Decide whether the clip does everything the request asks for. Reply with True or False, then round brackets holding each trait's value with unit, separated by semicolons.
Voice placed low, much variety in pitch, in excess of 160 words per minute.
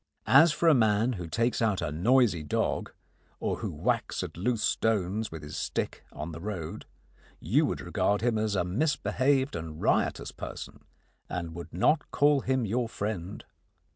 True (105 Hz; 6.4 semitones; 170 wpm)